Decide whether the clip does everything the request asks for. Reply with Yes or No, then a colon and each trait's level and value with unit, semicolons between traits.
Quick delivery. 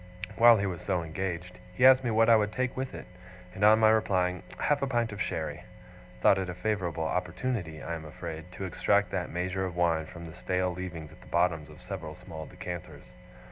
Yes: fast, 215 wpm